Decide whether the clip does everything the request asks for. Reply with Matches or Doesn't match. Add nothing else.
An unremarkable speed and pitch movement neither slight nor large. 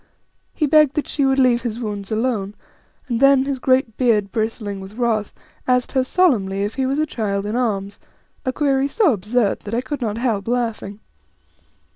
Matches